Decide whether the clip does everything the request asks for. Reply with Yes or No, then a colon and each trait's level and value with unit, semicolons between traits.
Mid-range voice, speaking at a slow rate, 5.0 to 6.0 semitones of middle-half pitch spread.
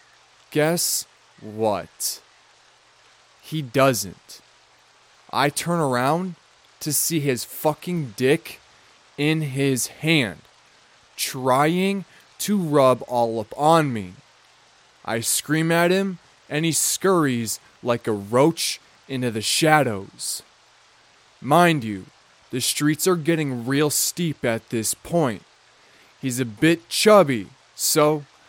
Yes: medium, 145 Hz; slow, 105 wpm; wide, 5.4 semitones